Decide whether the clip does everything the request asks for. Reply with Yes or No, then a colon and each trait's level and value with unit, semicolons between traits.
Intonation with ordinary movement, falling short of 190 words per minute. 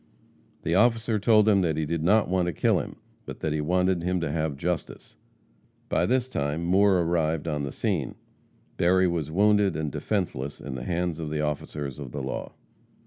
No: average, 4.1 semitones; average, 195 wpm